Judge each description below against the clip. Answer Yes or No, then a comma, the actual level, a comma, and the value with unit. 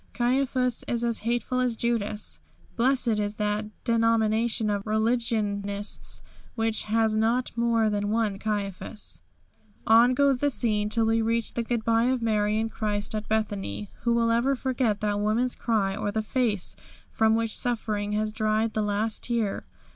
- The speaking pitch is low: No, high, 220 Hz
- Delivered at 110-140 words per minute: No, average, 155 wpm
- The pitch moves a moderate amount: No, narrow, 2.0 semitones